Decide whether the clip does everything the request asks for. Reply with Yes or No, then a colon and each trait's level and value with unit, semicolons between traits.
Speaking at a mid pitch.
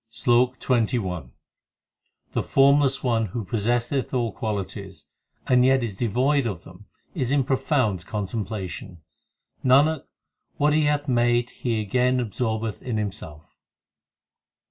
No: low, 120 Hz